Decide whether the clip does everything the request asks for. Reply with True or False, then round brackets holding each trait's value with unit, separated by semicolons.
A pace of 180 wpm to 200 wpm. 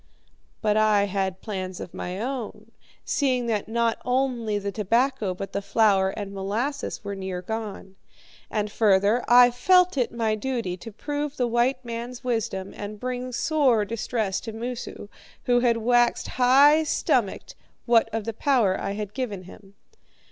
False (155 wpm)